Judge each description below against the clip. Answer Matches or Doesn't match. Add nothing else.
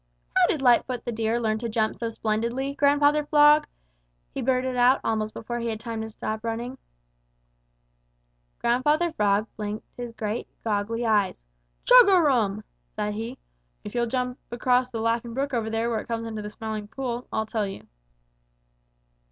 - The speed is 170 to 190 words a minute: Doesn't match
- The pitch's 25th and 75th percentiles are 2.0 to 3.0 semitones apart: Matches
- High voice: Matches